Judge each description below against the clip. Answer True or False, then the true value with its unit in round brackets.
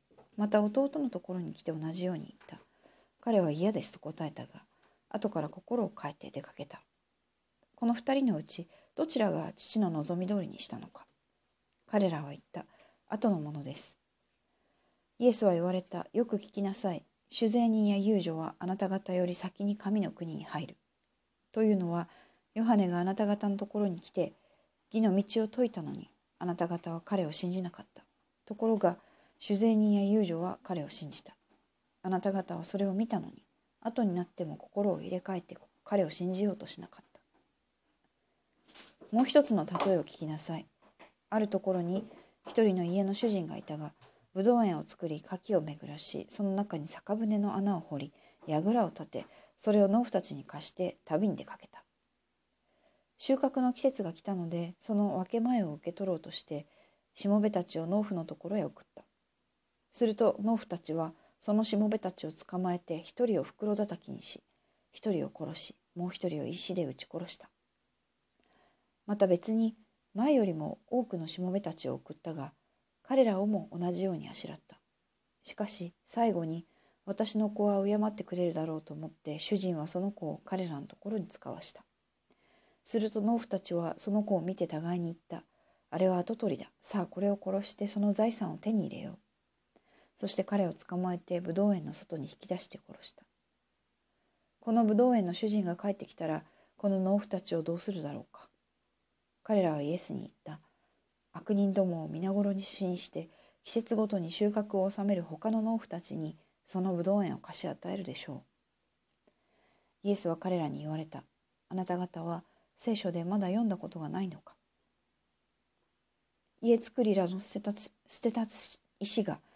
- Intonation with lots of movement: False (3.4 semitones)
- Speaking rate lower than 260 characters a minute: False (320 characters per minute)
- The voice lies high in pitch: True (195 Hz)